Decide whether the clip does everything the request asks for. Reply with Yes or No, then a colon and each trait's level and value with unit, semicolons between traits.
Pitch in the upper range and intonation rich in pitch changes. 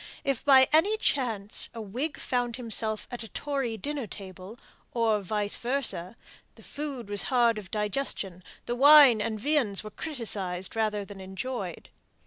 No: high, 230 Hz; average, 4.5 semitones